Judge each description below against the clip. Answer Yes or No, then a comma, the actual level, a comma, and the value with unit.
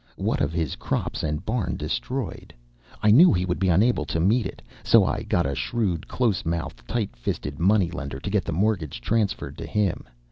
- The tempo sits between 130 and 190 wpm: No, average, 200 wpm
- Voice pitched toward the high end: No, very low, 90 Hz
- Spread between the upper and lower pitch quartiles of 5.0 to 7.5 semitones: Yes, average, 5.3 semitones